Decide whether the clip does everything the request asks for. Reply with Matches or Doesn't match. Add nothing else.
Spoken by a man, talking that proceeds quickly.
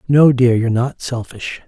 Doesn't match